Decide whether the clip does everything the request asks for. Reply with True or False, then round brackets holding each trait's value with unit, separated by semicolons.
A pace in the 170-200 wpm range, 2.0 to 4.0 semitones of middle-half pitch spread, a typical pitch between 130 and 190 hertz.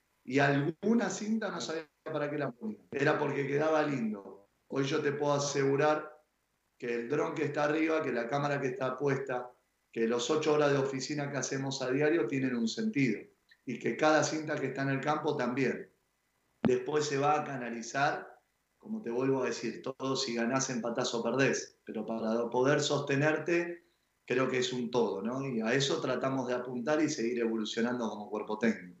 True (190 wpm; 3.3 semitones; 135 Hz)